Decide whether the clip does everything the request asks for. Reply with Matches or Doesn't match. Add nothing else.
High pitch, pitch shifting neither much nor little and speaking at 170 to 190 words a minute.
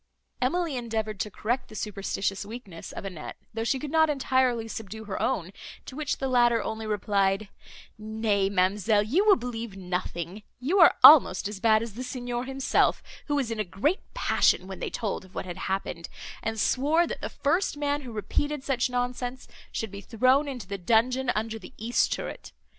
Matches